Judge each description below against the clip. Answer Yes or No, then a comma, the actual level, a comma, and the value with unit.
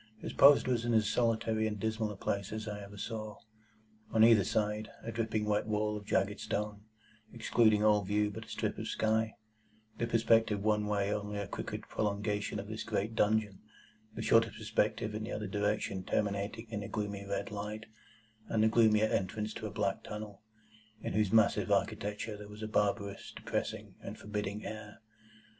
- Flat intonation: Yes, narrow, 1.2 semitones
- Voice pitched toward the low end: Yes, low, 105 Hz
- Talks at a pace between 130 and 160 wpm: No, average, 180 wpm